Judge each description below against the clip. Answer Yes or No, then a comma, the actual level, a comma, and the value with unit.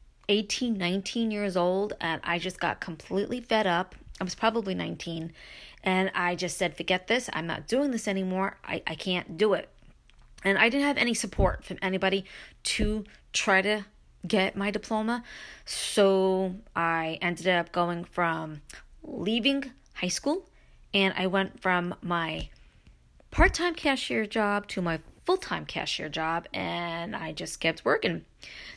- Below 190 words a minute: Yes, average, 155 wpm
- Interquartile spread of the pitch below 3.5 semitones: No, average, 3.8 semitones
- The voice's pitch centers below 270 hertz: Yes, high, 190 Hz